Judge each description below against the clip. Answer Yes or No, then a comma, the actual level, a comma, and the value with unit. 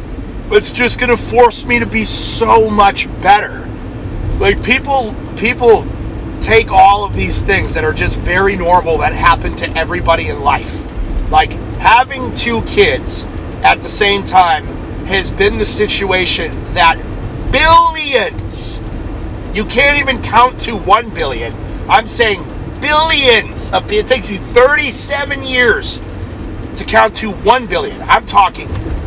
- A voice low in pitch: No, very high, 260 Hz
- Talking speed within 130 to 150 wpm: Yes, slow, 135 wpm